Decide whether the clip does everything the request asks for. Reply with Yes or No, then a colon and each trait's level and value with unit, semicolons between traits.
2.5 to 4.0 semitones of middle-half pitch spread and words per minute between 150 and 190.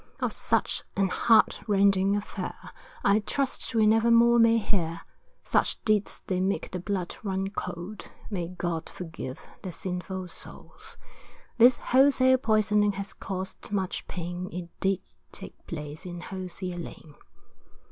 No: average, 3.1 semitones; slow, 135 wpm